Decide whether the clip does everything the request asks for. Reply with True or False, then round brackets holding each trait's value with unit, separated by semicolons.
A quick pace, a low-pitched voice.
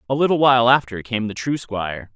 True (220 wpm; 115 Hz)